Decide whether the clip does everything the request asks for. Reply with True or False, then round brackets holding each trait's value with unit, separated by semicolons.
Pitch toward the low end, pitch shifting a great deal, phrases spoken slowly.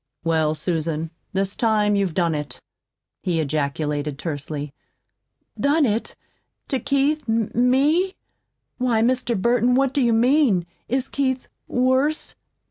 False (225 Hz; 8.2 semitones; 120 wpm)